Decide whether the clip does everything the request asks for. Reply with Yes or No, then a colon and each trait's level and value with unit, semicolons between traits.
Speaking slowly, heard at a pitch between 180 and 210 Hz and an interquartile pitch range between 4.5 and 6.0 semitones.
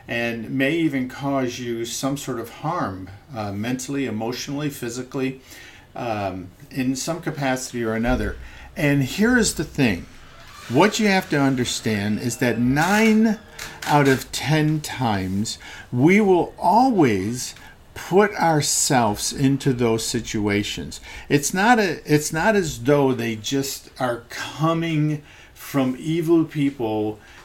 No: slow, 125 wpm; low, 135 Hz; average, 4.8 semitones